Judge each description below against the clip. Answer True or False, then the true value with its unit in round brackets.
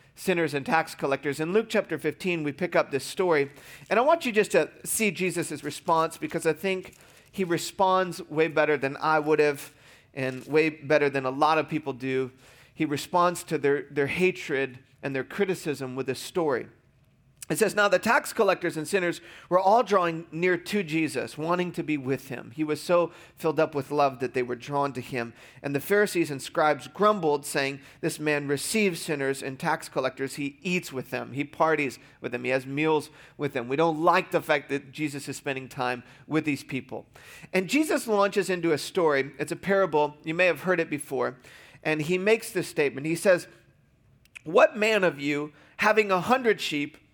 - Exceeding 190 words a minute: True (200 wpm)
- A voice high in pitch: False (155 Hz)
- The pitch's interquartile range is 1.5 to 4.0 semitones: False (4.4 semitones)